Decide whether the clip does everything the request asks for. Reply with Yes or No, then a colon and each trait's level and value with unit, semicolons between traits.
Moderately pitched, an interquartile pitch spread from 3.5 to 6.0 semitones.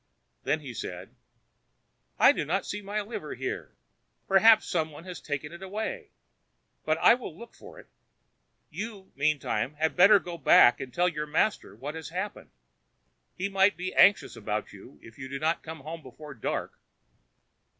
Yes: medium, 165 Hz; average, 5.0 semitones